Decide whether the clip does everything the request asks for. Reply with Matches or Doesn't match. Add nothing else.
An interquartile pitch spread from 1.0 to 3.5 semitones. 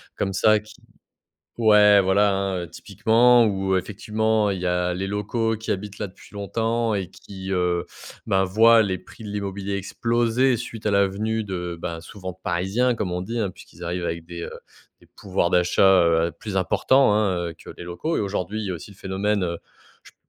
Matches